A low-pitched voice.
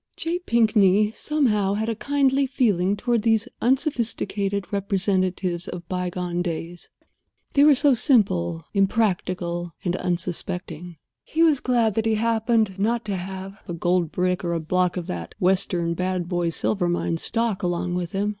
No: high, 195 Hz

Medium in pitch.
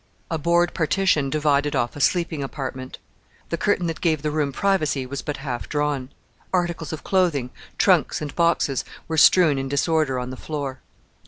Yes: medium, 150 Hz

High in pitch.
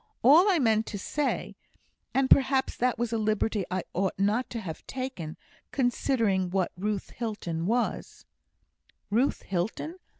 Yes: high, 225 Hz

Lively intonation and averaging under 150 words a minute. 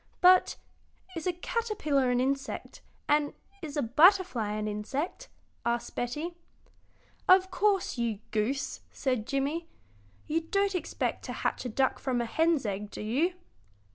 Yes: wide, 6.6 semitones; average, 140 wpm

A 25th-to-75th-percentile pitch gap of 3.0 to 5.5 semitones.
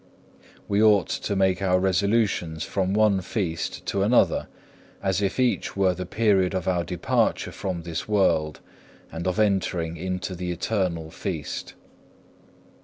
No: narrow, 2.4 semitones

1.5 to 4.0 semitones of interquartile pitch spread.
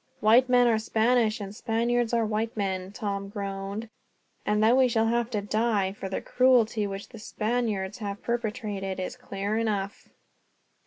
Yes: average, 2.8 semitones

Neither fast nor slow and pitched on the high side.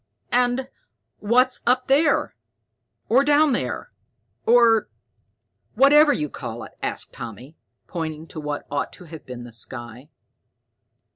No: slow, 125 wpm; high, 205 Hz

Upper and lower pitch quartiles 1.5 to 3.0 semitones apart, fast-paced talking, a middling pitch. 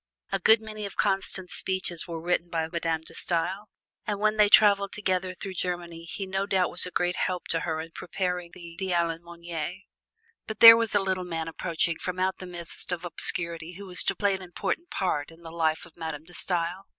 Yes: narrow, 2.4 semitones; fast, 210 wpm; medium, 180 Hz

